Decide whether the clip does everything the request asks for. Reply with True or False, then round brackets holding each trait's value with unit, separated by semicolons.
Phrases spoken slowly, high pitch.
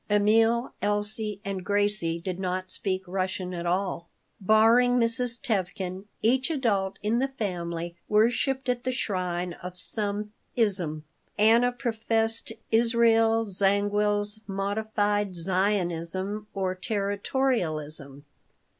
True (105 wpm; 205 Hz)